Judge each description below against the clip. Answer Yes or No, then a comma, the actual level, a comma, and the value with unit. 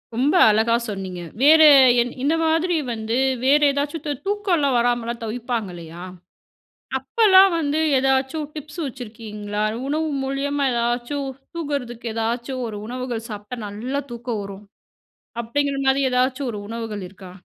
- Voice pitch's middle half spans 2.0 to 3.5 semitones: No, average, 4.2 semitones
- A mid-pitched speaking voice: No, very high, 250 Hz